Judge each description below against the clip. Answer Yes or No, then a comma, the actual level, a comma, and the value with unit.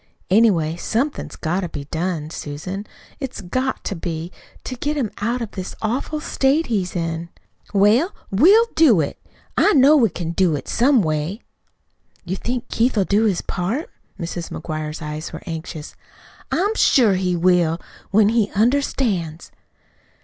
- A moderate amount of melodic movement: No, wide, 7.0 semitones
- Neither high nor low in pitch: No, high, 195 Hz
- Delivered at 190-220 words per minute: No, average, 150 wpm